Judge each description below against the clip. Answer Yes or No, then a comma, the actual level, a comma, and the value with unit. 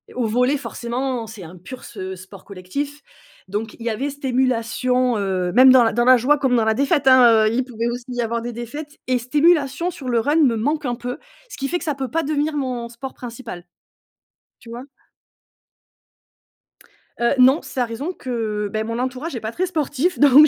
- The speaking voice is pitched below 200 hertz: No, very high, 250 Hz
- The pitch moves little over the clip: No, average, 3.4 semitones